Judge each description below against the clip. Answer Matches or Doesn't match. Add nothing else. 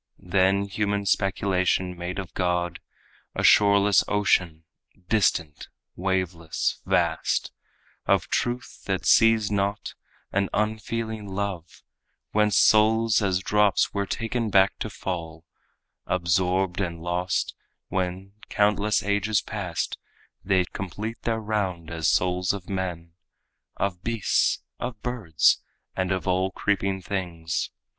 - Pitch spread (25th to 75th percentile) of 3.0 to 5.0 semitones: Doesn't match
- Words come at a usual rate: Doesn't match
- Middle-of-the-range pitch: Doesn't match